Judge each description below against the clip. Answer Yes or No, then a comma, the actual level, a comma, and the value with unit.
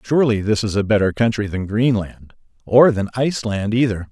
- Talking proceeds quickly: No, average, 175 wpm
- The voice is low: Yes, low, 110 Hz